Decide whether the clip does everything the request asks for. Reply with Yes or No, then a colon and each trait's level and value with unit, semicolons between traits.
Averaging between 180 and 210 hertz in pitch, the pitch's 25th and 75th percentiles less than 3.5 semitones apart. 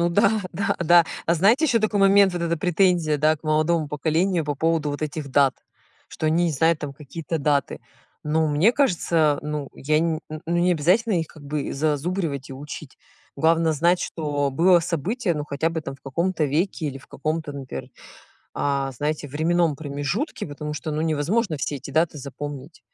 No: medium, 155 Hz; average, 3.0 semitones